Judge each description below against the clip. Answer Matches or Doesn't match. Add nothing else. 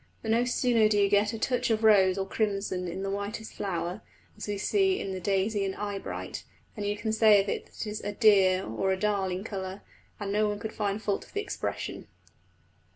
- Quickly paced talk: Matches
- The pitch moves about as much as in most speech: Doesn't match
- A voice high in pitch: Matches